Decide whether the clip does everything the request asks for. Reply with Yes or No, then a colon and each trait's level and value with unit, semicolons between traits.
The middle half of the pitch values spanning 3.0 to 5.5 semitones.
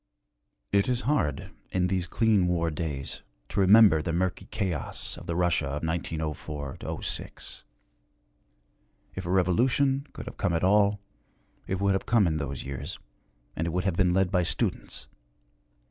Yes: average, 3.7 semitones